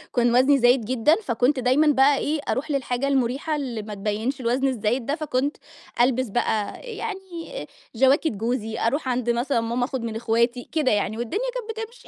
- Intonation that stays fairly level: No, average, 3.6 semitones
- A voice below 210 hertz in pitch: No, very high, 255 Hz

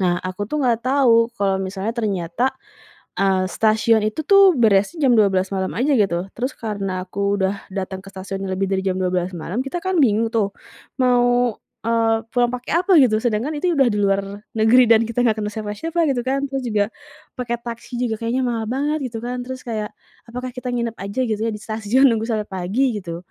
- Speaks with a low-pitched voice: No, high, 220 Hz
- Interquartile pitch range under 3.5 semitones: No, average, 3.9 semitones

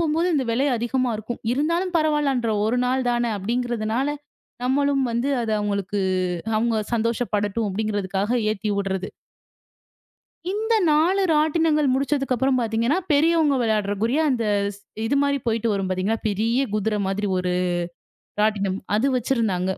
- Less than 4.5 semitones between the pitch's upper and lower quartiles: No, average, 5.0 semitones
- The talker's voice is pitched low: No, high, 235 Hz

